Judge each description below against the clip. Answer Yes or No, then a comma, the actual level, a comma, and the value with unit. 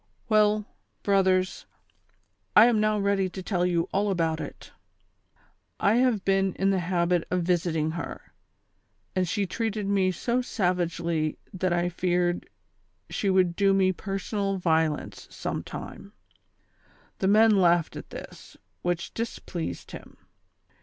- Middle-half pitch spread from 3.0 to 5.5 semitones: No, narrow, 2.5 semitones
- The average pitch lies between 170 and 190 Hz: Yes, medium, 185 Hz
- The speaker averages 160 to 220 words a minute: No, average, 140 wpm